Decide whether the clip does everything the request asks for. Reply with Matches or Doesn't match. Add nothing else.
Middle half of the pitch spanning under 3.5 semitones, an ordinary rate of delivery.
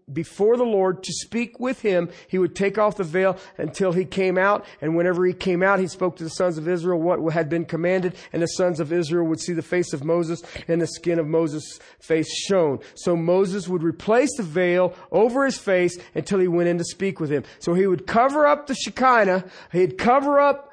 Doesn't match